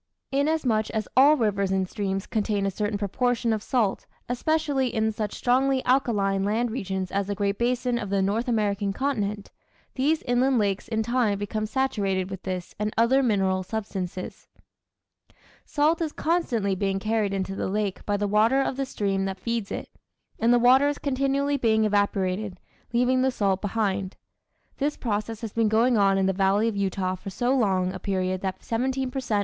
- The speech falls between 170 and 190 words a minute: Yes, average, 180 wpm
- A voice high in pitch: Yes, high, 215 Hz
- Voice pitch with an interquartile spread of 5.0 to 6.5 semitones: No, average, 4.2 semitones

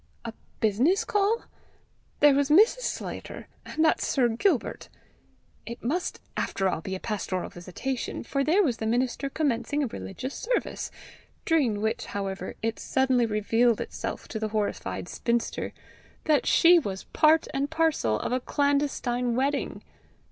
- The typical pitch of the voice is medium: No, very high, 255 Hz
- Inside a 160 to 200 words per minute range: No, average, 145 wpm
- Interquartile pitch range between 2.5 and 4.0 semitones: No, wide, 5.4 semitones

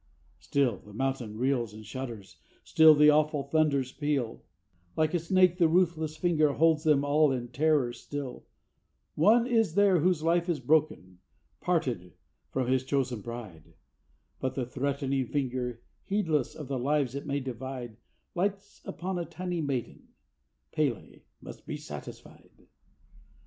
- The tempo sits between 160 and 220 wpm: No, average, 140 wpm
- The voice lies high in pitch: No, medium, 140 Hz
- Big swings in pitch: No, average, 4.2 semitones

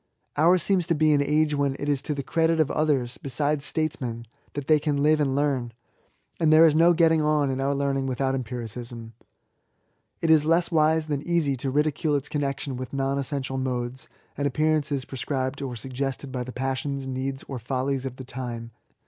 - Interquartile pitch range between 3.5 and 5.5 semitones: No, average, 2.7 semitones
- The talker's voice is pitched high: No, medium, 140 Hz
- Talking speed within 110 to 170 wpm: No, average, 190 wpm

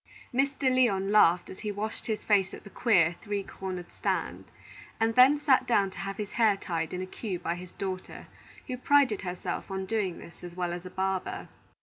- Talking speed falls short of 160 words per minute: No, fast, 205 wpm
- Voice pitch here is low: No, high, 195 Hz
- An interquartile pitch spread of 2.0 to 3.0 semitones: No, average, 3.6 semitones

